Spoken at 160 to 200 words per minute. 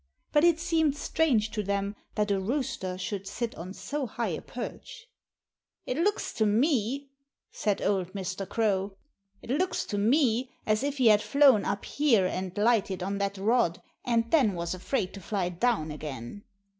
Yes: average, 170 wpm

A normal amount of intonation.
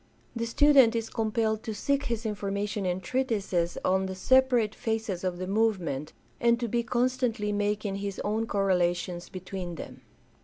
Yes: average, 3.6 semitones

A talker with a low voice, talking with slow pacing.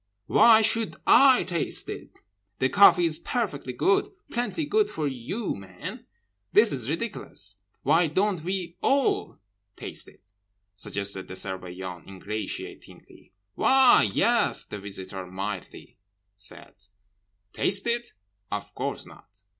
Yes: low, 125 Hz; slow, 110 wpm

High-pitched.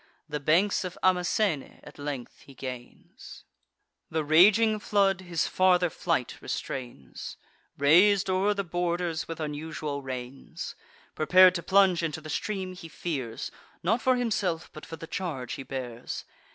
No: medium, 170 Hz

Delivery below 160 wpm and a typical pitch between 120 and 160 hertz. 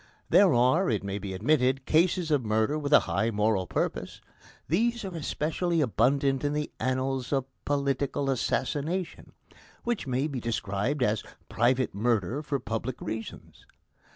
Yes: average, 145 wpm; low, 135 Hz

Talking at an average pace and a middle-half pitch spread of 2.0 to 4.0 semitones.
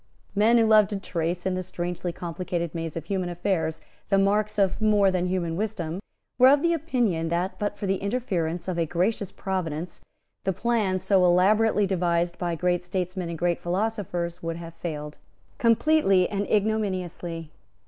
Yes: average, 165 wpm; average, 3.2 semitones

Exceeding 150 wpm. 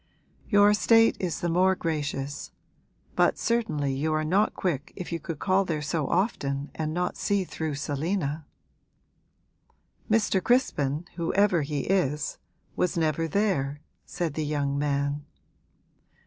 No: slow, 135 wpm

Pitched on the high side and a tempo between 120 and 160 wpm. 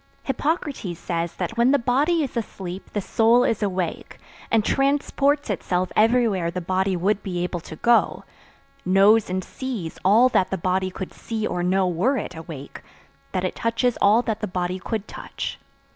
No: high, 200 Hz; average, 175 wpm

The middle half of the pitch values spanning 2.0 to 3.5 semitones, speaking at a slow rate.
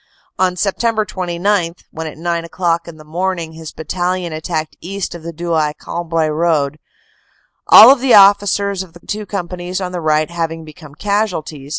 No: average, 2.9 semitones; average, 170 wpm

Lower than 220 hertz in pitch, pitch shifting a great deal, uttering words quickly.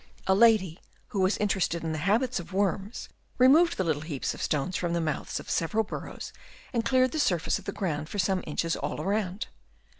No: high, 190 Hz; average, 4.7 semitones; fast, 210 wpm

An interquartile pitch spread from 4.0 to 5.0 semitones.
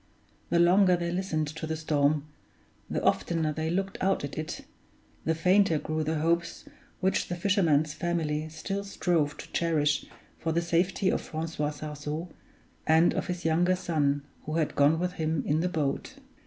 No: narrow, 2.5 semitones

